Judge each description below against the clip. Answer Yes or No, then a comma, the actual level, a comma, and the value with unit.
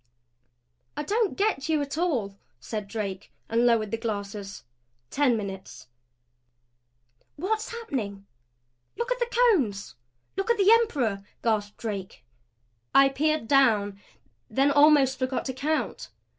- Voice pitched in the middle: No, very high, 260 Hz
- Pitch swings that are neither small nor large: No, wide, 7.3 semitones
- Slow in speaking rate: Yes, slow, 125 wpm